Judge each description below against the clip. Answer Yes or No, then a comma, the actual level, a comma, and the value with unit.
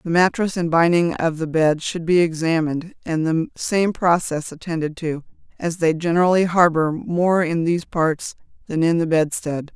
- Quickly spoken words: No, average, 170 wpm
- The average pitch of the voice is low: No, medium, 165 Hz